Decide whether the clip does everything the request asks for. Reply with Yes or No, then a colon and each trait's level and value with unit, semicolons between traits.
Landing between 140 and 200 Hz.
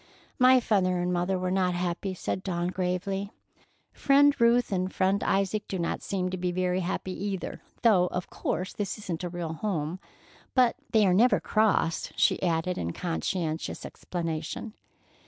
Yes: medium, 185 Hz